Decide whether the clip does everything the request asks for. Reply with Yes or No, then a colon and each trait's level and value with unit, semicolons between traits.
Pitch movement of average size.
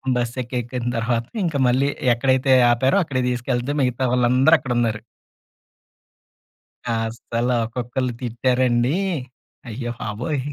No: narrow, 1.6 semitones